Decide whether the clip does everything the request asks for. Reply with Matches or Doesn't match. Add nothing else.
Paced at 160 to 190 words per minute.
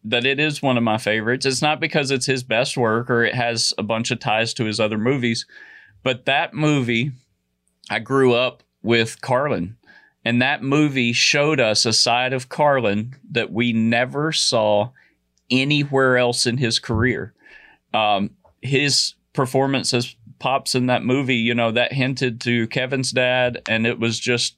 Matches